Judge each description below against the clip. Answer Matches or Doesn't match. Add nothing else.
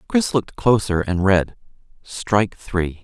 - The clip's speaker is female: Doesn't match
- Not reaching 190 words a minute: Matches